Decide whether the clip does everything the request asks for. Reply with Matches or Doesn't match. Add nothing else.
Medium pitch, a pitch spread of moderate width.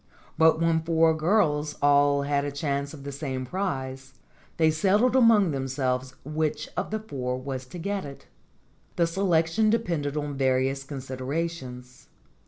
Matches